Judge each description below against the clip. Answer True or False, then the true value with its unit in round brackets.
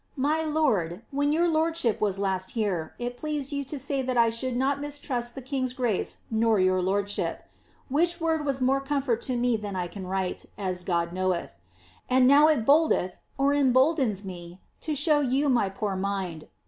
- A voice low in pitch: False (245 Hz)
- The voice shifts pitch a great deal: True (6.6 semitones)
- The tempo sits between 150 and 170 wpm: False (180 wpm)